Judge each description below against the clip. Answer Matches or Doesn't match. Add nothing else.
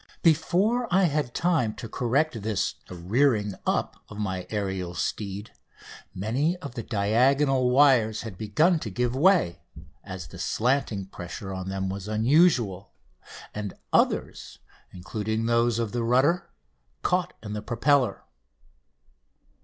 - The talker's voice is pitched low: Matches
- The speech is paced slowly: Matches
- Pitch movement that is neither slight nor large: Doesn't match